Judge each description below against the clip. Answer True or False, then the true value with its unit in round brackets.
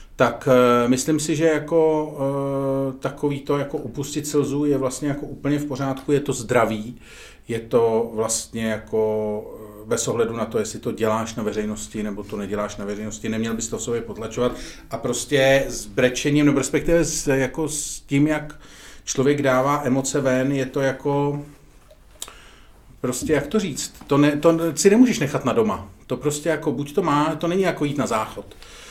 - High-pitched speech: False (135 Hz)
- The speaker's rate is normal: False (180 wpm)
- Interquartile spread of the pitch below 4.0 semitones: False (4.3 semitones)